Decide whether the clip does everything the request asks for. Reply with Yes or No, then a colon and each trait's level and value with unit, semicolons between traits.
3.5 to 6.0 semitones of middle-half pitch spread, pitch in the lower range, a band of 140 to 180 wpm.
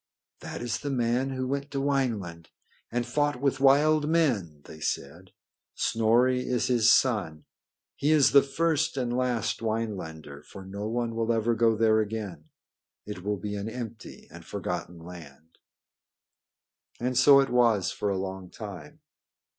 Yes: average, 5.1 semitones; low, 115 Hz; average, 155 wpm